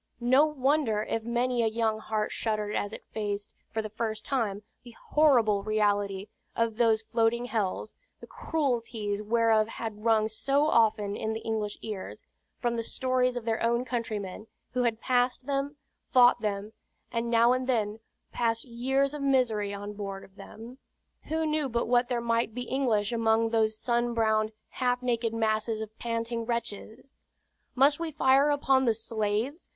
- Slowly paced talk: No, average, 165 wpm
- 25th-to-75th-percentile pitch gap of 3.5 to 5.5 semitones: No, narrow, 2.5 semitones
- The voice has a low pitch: No, high, 230 Hz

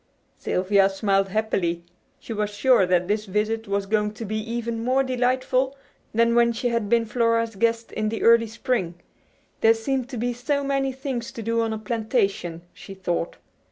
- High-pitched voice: Yes, high, 225 Hz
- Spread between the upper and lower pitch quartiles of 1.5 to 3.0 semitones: Yes, average, 2.7 semitones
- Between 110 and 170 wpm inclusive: No, average, 180 wpm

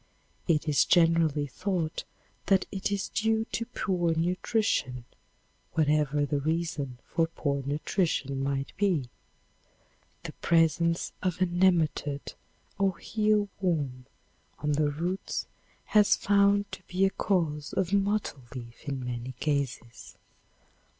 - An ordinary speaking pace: No, slow, 120 wpm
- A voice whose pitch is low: No, medium, 165 Hz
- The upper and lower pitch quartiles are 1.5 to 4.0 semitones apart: No, average, 5.0 semitones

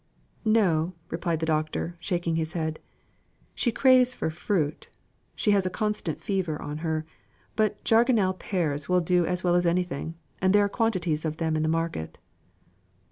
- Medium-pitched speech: Yes, medium, 175 Hz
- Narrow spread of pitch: No, average, 3.5 semitones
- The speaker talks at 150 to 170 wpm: Yes, average, 165 wpm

